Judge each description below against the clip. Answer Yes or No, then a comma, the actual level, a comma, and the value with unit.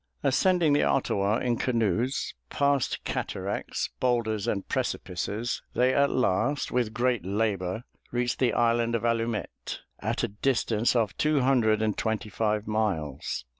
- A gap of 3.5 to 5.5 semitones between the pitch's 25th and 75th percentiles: No, average, 3.0 semitones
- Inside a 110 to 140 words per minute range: Yes, slow, 135 wpm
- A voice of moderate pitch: No, low, 115 Hz